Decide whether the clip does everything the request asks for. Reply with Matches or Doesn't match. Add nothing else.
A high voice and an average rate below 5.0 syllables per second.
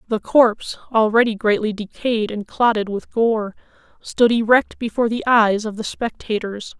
Matches